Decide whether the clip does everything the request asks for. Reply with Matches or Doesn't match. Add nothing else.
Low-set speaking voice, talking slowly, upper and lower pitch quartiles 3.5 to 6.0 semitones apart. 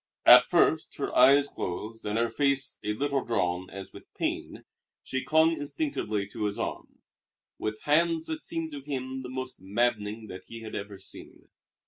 Doesn't match